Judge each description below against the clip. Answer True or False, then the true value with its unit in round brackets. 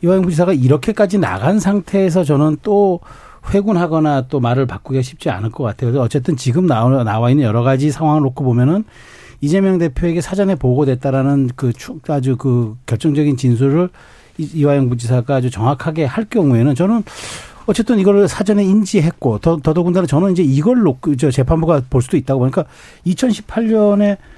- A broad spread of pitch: True (6.0 semitones)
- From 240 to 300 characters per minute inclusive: False (375 characters per minute)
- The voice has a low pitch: False (150 Hz)